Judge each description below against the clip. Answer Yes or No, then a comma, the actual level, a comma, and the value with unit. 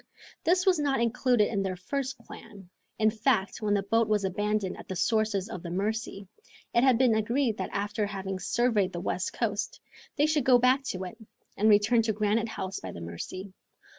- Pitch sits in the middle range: No, high, 215 Hz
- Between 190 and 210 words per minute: Yes, average, 195 wpm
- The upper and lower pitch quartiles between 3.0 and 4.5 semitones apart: Yes, average, 3.5 semitones